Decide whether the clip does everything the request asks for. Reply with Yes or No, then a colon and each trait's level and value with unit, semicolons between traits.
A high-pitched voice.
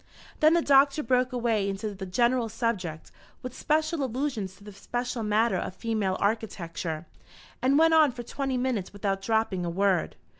Yes: high, 225 Hz